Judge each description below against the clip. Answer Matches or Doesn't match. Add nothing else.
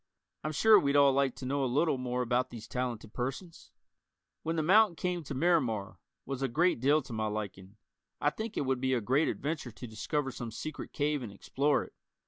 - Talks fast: Matches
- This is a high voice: Doesn't match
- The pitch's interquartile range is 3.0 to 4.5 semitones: Matches